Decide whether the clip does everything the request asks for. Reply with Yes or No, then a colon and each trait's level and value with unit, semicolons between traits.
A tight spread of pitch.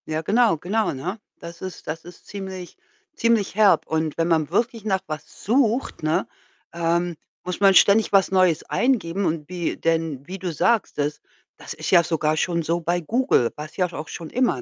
No: average, 3.9 semitones